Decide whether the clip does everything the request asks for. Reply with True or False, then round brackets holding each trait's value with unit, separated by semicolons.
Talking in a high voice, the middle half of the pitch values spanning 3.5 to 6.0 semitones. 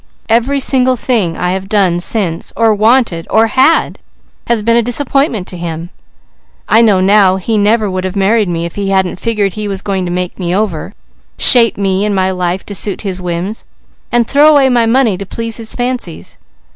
True (205 Hz; 3.8 semitones)